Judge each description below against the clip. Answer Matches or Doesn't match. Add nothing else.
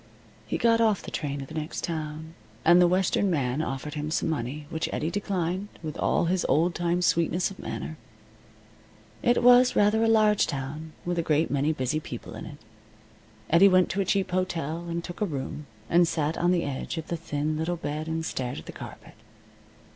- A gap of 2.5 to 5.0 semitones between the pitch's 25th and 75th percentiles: Matches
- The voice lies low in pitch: Doesn't match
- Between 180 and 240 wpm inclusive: Matches